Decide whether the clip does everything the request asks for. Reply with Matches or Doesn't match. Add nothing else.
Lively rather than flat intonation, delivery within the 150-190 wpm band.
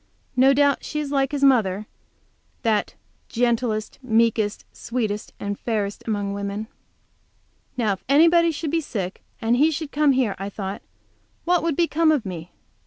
Matches